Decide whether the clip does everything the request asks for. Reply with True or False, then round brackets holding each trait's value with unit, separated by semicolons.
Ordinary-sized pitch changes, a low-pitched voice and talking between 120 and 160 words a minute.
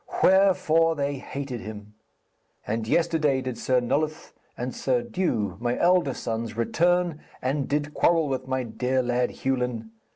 True (4.4 semitones; 130 Hz; 140 wpm)